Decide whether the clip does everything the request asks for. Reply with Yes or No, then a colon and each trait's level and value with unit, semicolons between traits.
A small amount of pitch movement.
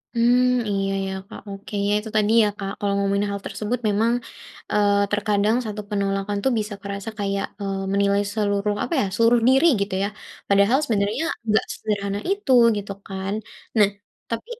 Yes: narrow, 1.8 semitones